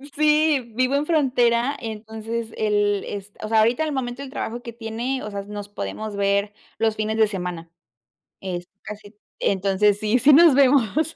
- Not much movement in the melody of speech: No, average, 4.0 semitones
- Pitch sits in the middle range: No, high, 220 Hz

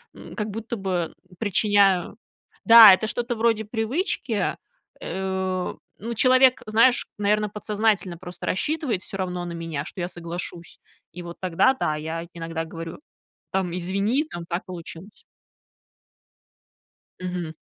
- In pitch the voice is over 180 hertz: Yes, high, 190 Hz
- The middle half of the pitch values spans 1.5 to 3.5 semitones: No, average, 4.1 semitones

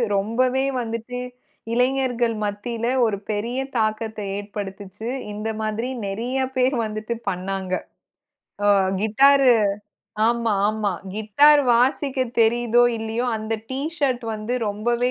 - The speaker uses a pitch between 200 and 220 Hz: No, high, 230 Hz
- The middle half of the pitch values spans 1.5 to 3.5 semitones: Yes, average, 2.7 semitones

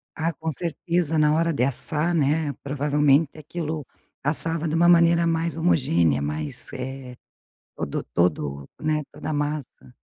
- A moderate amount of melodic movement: Yes, average, 3.4 semitones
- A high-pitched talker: No, medium, 150 Hz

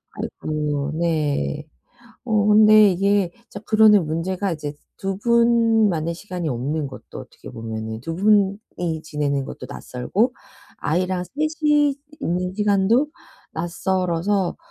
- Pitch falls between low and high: Yes, medium, 180 Hz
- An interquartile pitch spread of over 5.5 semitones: No, average, 5.2 semitones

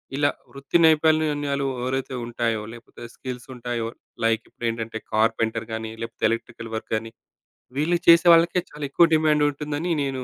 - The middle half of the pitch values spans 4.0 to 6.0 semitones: Yes, average, 4.7 semitones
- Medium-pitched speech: No, low, 130 Hz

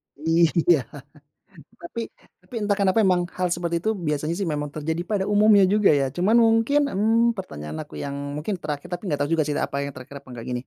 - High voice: No, medium, 175 Hz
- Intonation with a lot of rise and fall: Yes, wide, 5.8 semitones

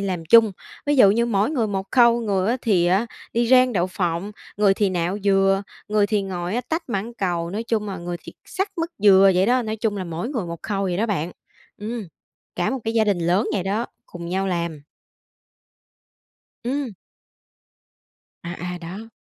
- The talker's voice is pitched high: Yes, high, 200 Hz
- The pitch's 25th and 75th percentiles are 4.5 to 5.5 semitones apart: No, average, 4.1 semitones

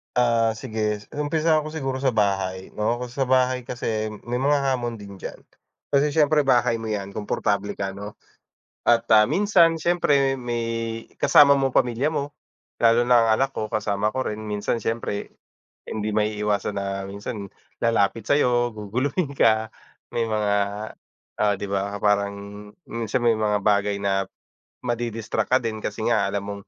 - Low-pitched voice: Yes, low, 115 Hz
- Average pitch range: Yes, average, 3.8 semitones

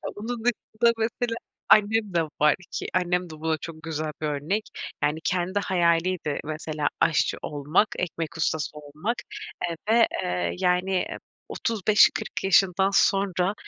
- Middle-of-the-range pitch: Yes, medium, 180 Hz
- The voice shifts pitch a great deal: No, average, 4.5 semitones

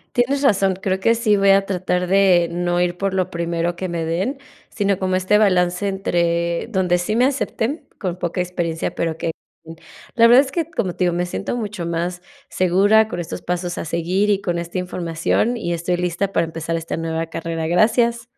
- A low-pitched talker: No, medium, 180 Hz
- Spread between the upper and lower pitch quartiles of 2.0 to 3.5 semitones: Yes, average, 2.9 semitones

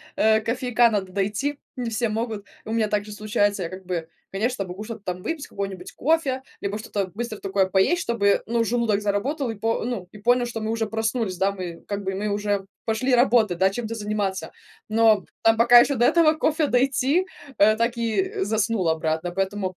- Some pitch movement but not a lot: Yes, average, 3.3 semitones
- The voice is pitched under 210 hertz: No, high, 215 Hz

